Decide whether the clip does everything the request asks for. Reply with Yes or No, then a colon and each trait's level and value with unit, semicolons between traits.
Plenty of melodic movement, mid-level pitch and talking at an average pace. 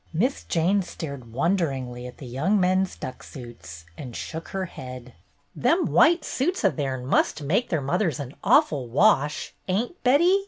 Yes: wide, 7.4 semitones; medium, 160 Hz; average, 160 wpm